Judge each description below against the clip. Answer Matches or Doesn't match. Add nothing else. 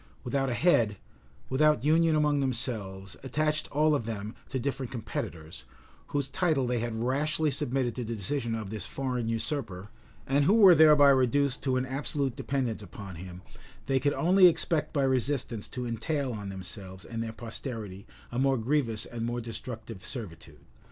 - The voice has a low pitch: Matches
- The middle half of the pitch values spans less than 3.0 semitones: Doesn't match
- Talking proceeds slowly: Doesn't match